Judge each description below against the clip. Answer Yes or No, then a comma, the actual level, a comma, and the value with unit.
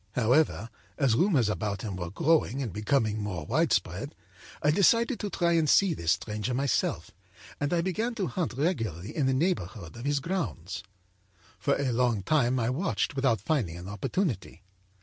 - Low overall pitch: Yes, low, 130 Hz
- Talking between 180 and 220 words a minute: No, average, 170 wpm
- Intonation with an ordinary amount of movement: No, wide, 7.4 semitones